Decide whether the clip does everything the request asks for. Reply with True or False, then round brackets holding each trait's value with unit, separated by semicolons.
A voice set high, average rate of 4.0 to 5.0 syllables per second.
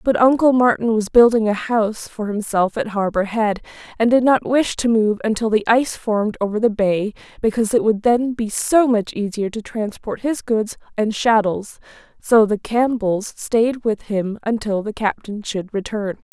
True (220 Hz; 4.7 syllables/s)